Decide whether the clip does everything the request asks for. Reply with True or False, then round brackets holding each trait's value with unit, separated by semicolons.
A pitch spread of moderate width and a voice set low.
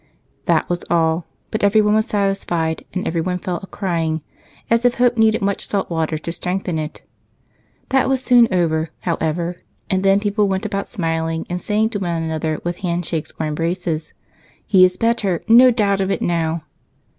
False (4.0 semitones; 180 Hz)